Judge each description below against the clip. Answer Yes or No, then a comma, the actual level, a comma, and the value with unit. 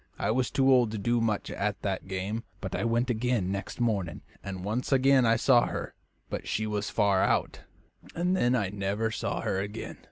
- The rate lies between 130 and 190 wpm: No, average, 200 wpm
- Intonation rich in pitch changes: No, average, 3.7 semitones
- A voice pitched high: No, low, 110 Hz